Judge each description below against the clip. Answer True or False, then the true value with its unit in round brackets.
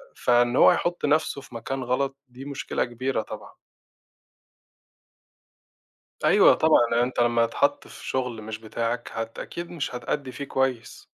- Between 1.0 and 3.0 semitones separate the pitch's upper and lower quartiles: True (2.6 semitones)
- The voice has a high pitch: False (125 Hz)